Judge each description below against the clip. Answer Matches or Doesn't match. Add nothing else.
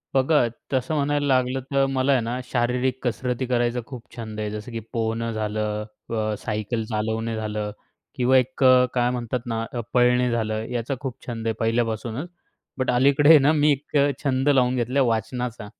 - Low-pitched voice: Matches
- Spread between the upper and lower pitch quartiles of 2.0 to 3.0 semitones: Matches